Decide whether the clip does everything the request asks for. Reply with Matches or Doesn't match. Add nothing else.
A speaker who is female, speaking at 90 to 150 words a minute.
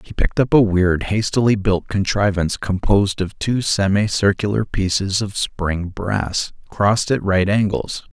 Doesn't match